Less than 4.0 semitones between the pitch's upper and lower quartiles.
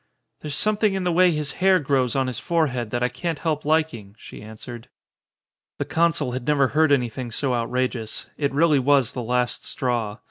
No: average, 4.4 semitones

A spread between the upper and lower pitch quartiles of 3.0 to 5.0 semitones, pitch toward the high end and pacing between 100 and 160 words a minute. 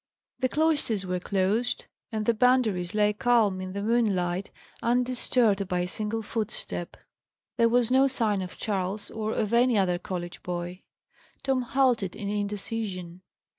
Yes: average, 4.3 semitones; high, 210 Hz; average, 145 wpm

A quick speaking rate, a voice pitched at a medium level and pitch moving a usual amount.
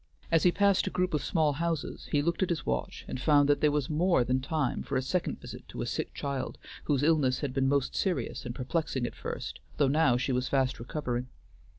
Yes: fast, 230 wpm; medium, 145 Hz; average, 3.8 semitones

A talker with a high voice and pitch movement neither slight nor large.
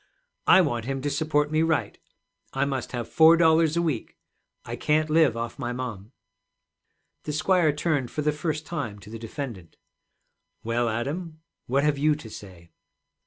No: medium, 145 Hz; average, 4.8 semitones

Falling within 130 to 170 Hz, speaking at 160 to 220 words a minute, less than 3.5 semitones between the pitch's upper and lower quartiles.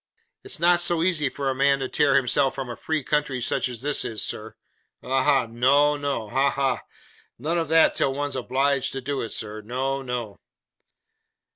Yes: low, 135 Hz; average, 190 wpm; narrow, 2.5 semitones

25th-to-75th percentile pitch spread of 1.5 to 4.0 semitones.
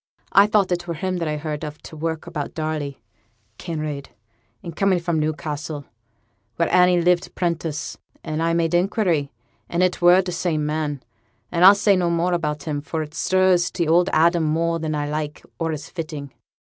Yes: narrow, 2.5 semitones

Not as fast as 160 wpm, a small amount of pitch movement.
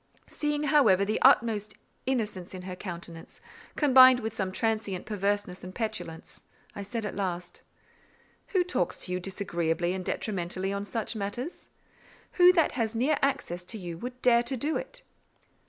No: average, 150 wpm; wide, 5.4 semitones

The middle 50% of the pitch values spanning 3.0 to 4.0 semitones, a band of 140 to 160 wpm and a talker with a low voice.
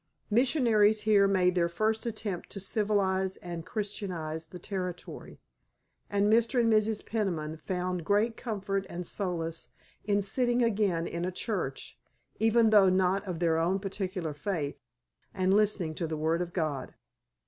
No: average, 3.6 semitones; average, 150 wpm; high, 190 Hz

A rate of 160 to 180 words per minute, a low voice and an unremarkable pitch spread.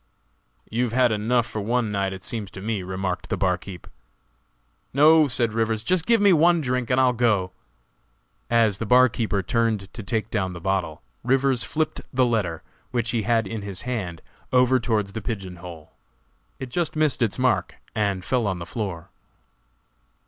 Yes: average, 175 wpm; low, 115 Hz; average, 4.5 semitones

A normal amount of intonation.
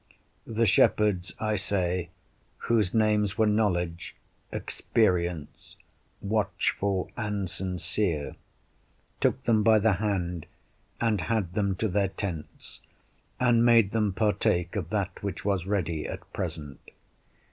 Yes: average, 3.3 semitones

